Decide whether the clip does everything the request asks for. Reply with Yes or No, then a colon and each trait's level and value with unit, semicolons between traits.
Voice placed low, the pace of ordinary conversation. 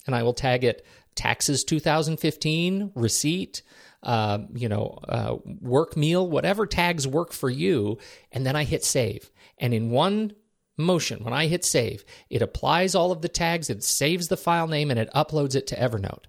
No: medium, 150 Hz; average, 180 wpm